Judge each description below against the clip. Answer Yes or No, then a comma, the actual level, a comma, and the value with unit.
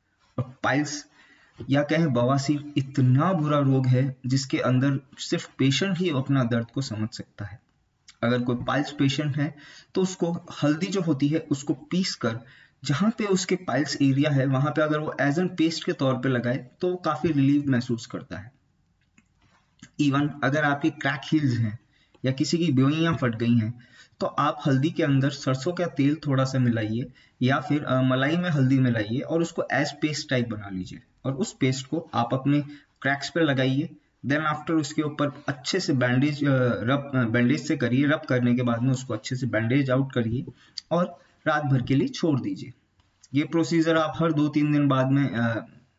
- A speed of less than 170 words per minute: No, average, 185 wpm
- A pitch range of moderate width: Yes, average, 3.3 semitones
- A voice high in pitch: No, medium, 140 Hz